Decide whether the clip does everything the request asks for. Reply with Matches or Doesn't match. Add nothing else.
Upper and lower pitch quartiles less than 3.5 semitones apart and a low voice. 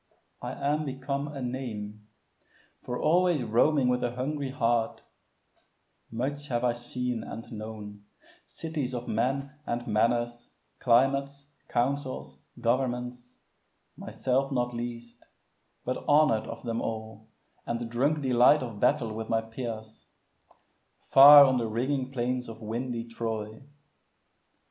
Matches